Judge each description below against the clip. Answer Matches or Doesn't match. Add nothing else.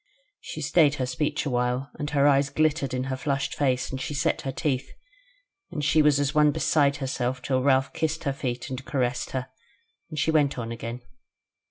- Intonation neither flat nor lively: Doesn't match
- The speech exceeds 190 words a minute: Matches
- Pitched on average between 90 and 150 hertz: Matches